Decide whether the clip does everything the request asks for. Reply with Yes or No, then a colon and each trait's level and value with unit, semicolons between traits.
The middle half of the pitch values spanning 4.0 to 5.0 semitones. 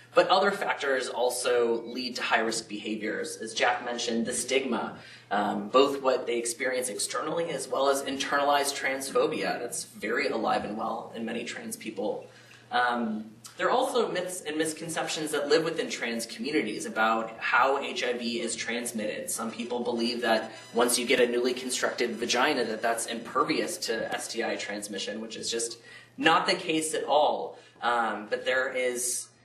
No: average, 3.0 semitones